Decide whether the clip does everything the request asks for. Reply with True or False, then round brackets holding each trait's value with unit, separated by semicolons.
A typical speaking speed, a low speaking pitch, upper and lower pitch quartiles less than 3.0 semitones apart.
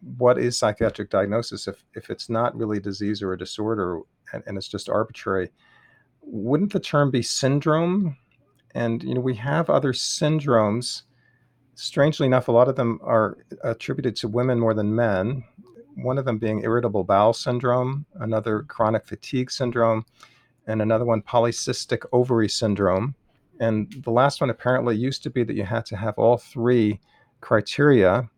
True (160 wpm; 120 Hz; 2.6 semitones)